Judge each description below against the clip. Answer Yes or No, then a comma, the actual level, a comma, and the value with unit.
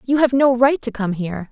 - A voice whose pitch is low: No, high, 240 Hz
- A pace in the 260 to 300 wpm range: Yes, fast, 275 wpm